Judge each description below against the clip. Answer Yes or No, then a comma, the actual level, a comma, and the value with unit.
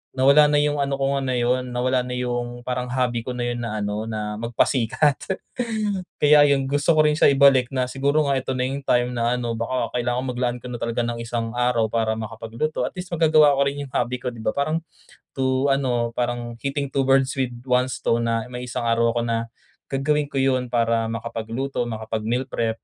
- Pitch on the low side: Yes, low, 125 Hz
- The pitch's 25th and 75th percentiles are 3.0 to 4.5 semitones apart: No, narrow, 2.6 semitones